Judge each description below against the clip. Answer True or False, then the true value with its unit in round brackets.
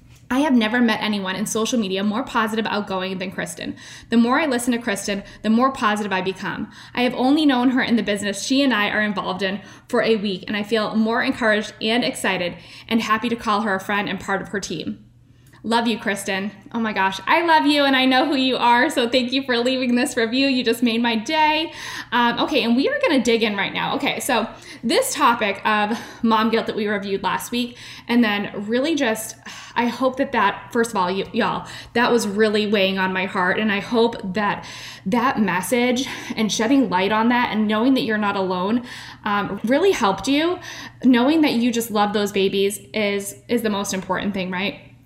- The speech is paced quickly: True (220 wpm)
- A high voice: True (220 Hz)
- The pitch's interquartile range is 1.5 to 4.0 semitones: True (3.7 semitones)